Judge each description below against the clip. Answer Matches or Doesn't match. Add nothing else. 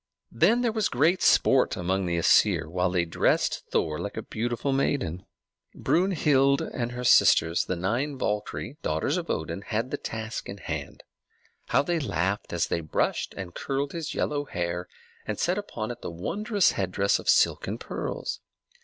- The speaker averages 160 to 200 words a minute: Matches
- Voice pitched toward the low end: Matches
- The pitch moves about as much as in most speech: Doesn't match